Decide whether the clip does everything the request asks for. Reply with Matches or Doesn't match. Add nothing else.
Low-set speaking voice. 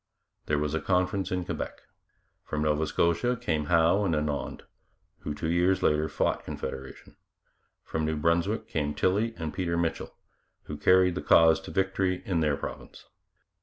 Matches